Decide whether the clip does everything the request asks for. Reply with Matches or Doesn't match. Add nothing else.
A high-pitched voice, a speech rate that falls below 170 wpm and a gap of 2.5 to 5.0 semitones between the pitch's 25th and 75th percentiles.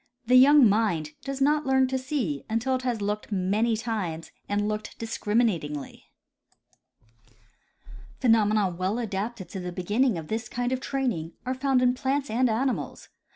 Matches